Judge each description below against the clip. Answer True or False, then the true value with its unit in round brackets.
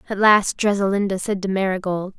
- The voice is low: False (195 Hz)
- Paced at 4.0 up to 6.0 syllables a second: True (5.6 syllables/s)